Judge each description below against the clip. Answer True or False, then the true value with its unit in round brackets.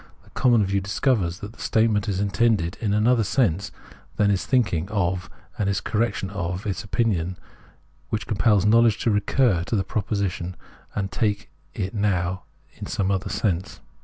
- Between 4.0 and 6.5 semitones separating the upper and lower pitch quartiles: False (2.8 semitones)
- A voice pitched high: False (100 Hz)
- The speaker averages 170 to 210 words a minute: False (160 wpm)